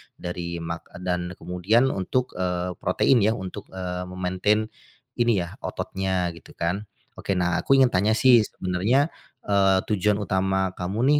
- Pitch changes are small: No, average, 3.1 semitones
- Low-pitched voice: Yes, very low, 95 Hz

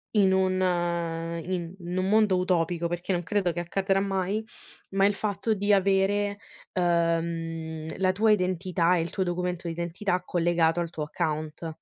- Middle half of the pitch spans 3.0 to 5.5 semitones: No, narrow, 2.4 semitones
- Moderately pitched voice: Yes, medium, 180 Hz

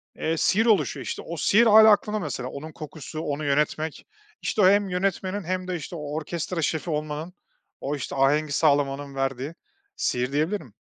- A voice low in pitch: No, medium, 155 Hz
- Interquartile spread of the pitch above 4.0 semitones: Yes, average, 4.5 semitones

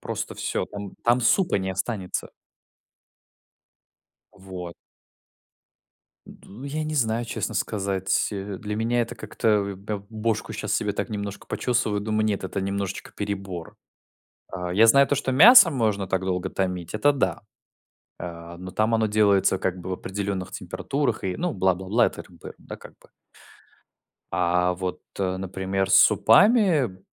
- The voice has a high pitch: No, low, 100 Hz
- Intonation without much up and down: No, average, 3.2 semitones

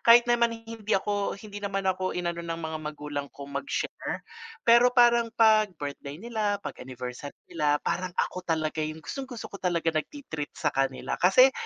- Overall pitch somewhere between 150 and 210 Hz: Yes, medium, 185 Hz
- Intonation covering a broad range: Yes, wide, 6.8 semitones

